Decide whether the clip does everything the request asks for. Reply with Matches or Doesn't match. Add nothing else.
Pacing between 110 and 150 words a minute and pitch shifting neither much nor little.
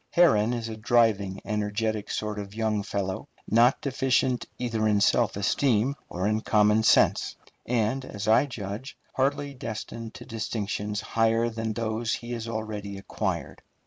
Doesn't match